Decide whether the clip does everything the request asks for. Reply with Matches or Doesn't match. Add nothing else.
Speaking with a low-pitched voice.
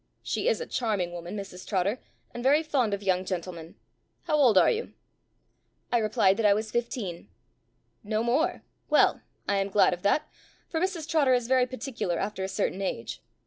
Doesn't match